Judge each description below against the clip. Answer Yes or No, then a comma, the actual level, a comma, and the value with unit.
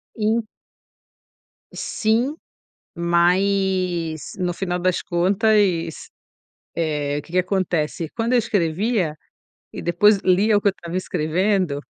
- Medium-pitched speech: Yes, medium, 180 Hz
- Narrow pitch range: No, average, 3.3 semitones